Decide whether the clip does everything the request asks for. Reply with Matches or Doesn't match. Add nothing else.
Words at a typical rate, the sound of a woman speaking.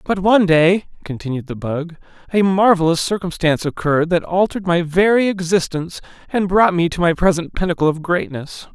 Doesn't match